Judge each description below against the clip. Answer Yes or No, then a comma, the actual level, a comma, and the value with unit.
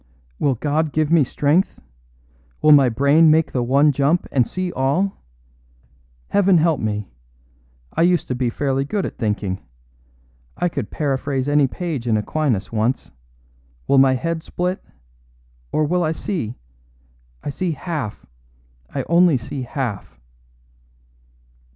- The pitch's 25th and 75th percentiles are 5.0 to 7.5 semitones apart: No, average, 4.5 semitones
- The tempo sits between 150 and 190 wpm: No, slow, 135 wpm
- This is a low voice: No, medium, 145 Hz